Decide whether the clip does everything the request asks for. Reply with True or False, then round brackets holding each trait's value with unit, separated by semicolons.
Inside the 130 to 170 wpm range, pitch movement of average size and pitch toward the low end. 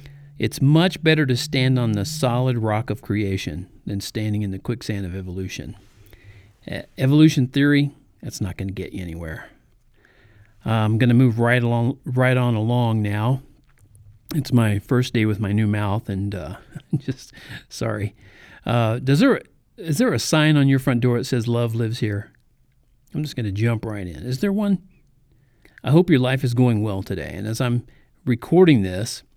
False (180 wpm; 4.1 semitones; 120 Hz)